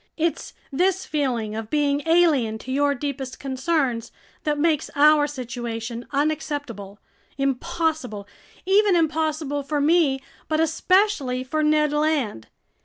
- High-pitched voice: Yes, very high, 290 Hz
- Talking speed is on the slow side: Yes, slow, 115 wpm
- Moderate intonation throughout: Yes, average, 3.7 semitones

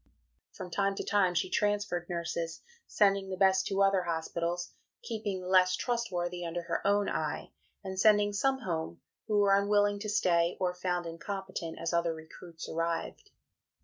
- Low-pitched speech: No, medium, 185 Hz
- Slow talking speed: No, average, 160 wpm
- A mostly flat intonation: No, average, 3.0 semitones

